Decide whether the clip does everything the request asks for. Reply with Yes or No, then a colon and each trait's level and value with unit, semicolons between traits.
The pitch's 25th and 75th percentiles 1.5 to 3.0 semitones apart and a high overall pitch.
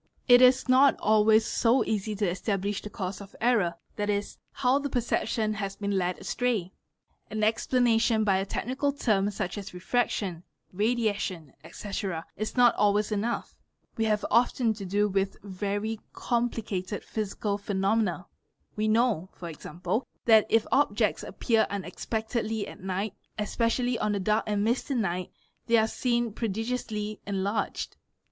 Yes: average, 2.7 semitones; high, 215 Hz